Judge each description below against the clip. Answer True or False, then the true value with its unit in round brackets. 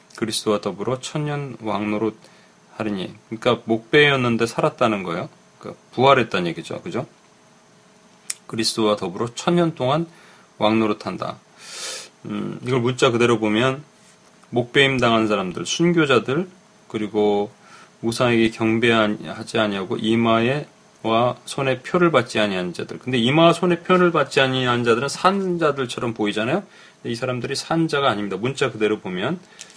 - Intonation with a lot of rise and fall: True (7.0 semitones)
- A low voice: True (125 Hz)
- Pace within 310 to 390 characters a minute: True (325 characters per minute)